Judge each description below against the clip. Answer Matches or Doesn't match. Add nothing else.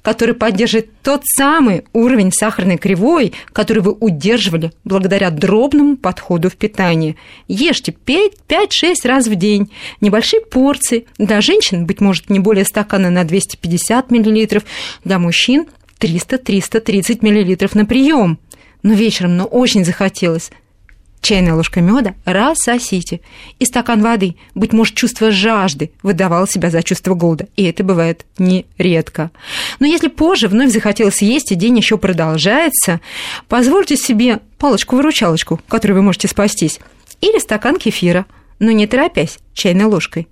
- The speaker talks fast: Doesn't match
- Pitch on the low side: Doesn't match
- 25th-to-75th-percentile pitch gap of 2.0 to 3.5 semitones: Doesn't match